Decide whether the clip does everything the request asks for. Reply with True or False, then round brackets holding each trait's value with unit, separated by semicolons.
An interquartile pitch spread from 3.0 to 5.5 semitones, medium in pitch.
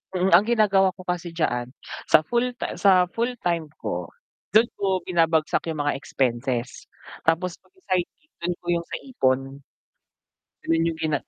True (3.7 semitones; 170 Hz)